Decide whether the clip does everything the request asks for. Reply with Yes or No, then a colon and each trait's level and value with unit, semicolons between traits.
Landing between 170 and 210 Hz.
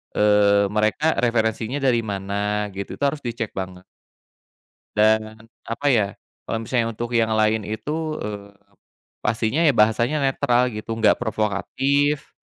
No: low, 110 Hz